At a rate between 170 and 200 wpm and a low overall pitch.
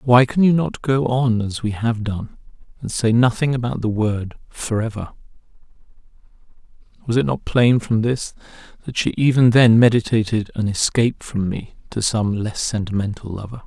No: average, 160 wpm; low, 115 Hz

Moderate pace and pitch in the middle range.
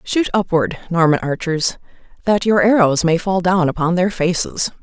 Yes: average, 160 wpm; medium, 180 Hz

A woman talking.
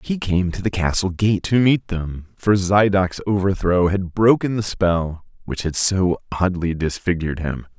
No: male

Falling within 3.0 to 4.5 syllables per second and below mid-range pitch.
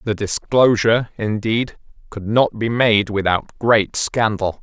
Yes: 3.9 syllables/s; low, 110 Hz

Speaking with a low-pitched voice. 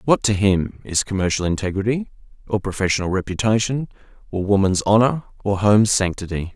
Yes: low, 100 Hz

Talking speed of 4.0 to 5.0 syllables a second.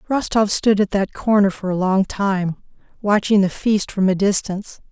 Yes: 4.7 syllables/s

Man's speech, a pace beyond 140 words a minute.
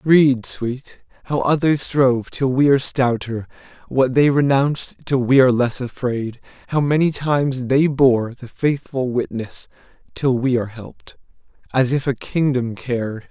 Yes: male; average, 155 wpm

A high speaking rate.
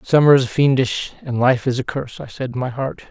Yes: fast, 250 wpm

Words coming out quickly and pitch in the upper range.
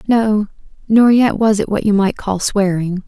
No: average, 195 wpm; high, 205 Hz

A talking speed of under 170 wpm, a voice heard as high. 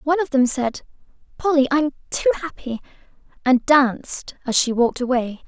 Yes: average, 155 wpm; very high, 270 Hz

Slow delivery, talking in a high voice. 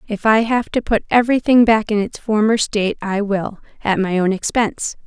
No: average, 200 wpm; high, 215 Hz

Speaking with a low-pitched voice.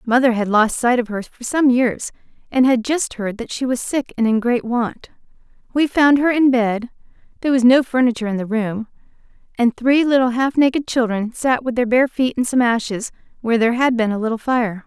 No: high, 245 Hz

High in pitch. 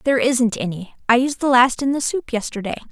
Yes: very high, 250 Hz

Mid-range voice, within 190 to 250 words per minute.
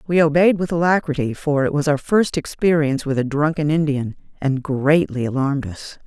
No: medium, 150 Hz; average, 180 wpm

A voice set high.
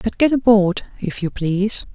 Yes: high, 205 Hz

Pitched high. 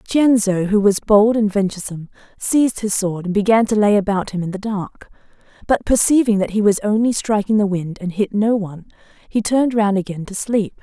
Yes: high, 205 Hz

